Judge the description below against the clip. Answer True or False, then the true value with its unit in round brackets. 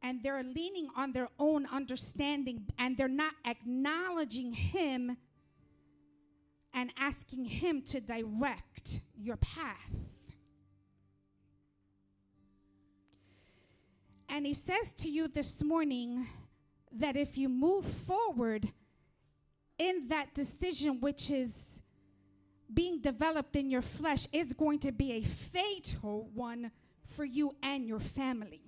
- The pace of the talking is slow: True (110 wpm)